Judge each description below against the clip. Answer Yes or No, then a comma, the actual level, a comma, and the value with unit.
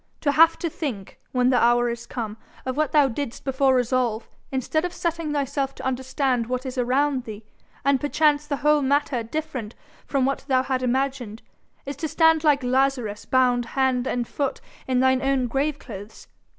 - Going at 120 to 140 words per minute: No, average, 175 wpm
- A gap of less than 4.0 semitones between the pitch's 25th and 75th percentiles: Yes, narrow, 2.6 semitones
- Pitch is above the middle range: Yes, very high, 265 Hz